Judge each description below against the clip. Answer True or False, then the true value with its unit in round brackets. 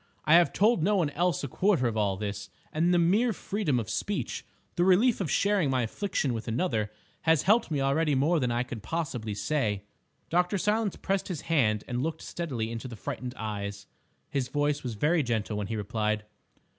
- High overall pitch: False (140 Hz)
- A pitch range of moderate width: False (7.7 semitones)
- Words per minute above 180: True (190 wpm)